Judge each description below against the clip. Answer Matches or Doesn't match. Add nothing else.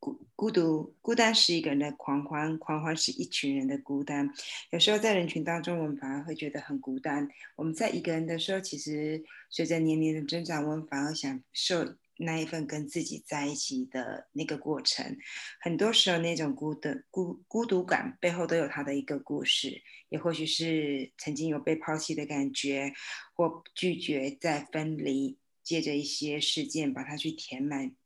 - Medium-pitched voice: Matches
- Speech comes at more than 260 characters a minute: Matches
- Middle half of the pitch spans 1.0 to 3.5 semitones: Matches